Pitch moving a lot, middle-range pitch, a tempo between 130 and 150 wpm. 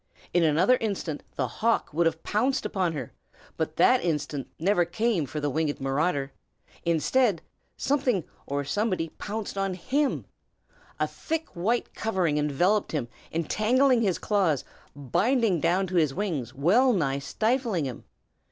Yes: wide, 6.6 semitones; medium, 180 Hz; average, 140 wpm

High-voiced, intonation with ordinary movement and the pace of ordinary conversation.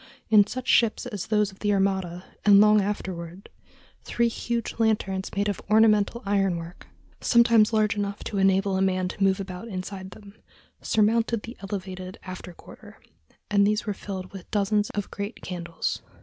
No: high, 200 Hz; narrow, 2.0 semitones; average, 165 wpm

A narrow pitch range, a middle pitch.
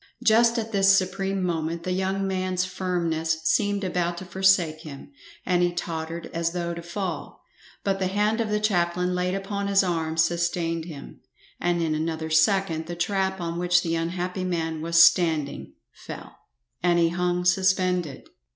Yes: narrow, 2.3 semitones; medium, 175 Hz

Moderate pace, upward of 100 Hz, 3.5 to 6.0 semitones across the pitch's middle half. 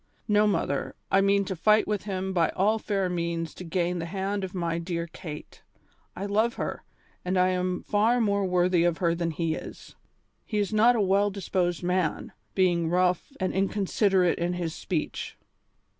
No: average, 180 wpm; medium, 185 Hz; average, 2.7 semitones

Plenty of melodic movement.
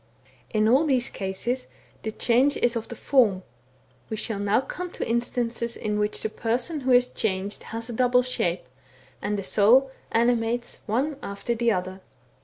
No: average, 3.1 semitones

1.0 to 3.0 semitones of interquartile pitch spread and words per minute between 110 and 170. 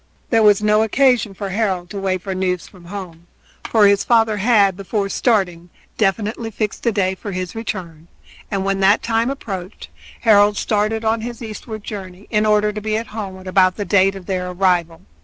No: narrow, 2.6 semitones; average, 190 wpm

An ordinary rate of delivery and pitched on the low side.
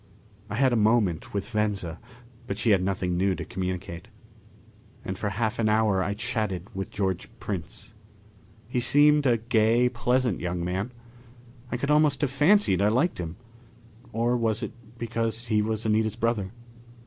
Yes: average, 160 wpm; low, 110 Hz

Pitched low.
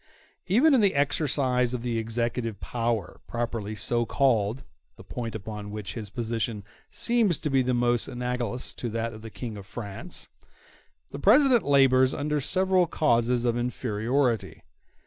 Yes: low, 120 Hz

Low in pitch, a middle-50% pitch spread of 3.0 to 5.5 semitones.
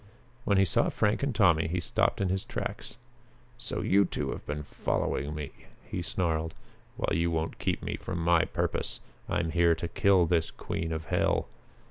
No: very low, 85 Hz; narrow, 2.6 semitones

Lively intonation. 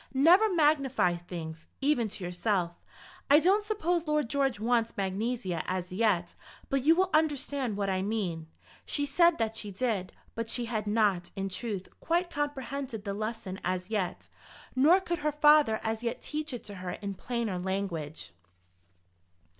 Yes: wide, 7.5 semitones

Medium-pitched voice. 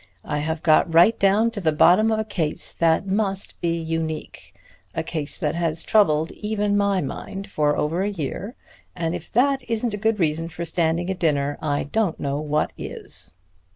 Yes: medium, 170 Hz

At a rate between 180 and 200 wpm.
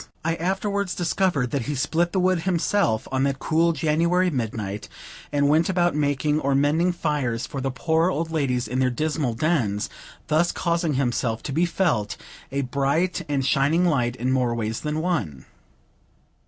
No: average, 170 wpm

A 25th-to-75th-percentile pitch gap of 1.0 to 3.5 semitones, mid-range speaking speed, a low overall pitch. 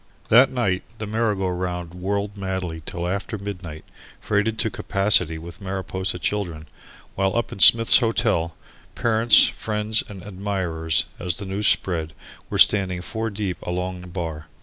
Yes: average, 3.0 semitones; average, 150 wpm; very low, 95 Hz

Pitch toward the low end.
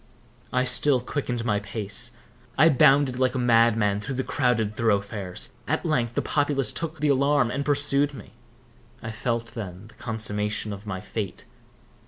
Yes: low, 120 Hz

